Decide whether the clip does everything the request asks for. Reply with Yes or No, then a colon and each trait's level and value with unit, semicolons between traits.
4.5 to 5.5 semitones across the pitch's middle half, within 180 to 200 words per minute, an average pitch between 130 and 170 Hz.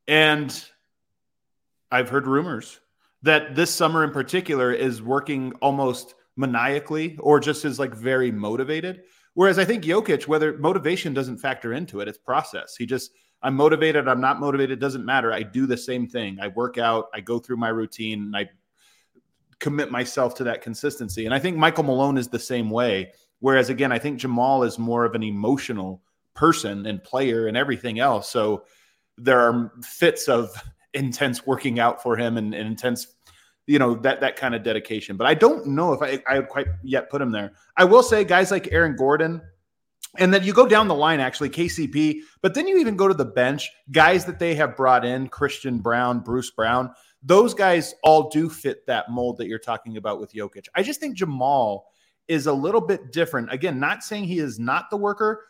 Yes: average, 4.8 semitones; average, 195 wpm; low, 135 Hz